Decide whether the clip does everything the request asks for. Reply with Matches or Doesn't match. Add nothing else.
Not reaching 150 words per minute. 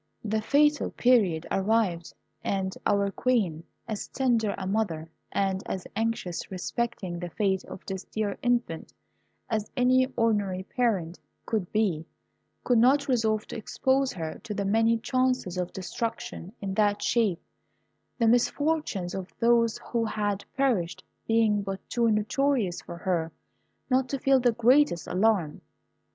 Matches